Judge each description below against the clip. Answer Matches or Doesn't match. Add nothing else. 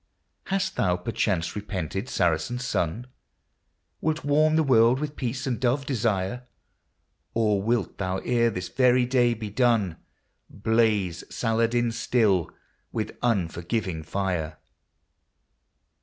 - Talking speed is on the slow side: Matches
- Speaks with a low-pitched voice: Matches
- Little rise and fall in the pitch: Doesn't match